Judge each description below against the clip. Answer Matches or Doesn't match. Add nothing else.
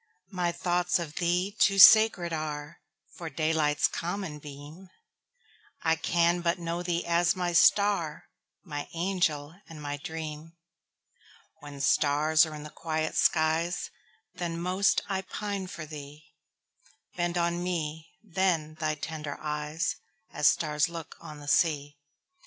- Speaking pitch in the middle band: Matches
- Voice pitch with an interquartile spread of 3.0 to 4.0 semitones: Doesn't match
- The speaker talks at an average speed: Doesn't match